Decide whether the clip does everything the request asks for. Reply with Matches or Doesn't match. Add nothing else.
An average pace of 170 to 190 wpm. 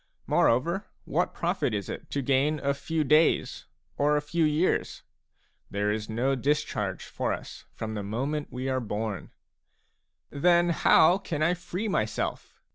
Doesn't match